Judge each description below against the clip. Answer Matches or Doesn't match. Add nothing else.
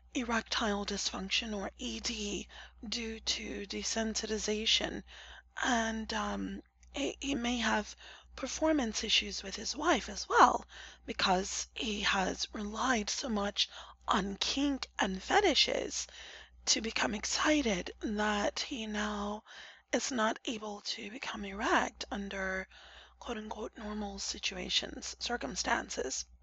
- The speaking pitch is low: Doesn't match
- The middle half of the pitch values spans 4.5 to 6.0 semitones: Doesn't match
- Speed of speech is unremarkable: Doesn't match